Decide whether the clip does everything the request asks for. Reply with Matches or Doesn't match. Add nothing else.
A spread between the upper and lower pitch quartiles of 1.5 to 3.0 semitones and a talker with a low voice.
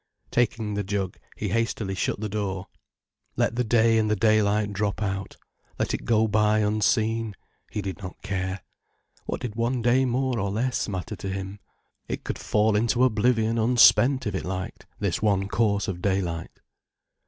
Matches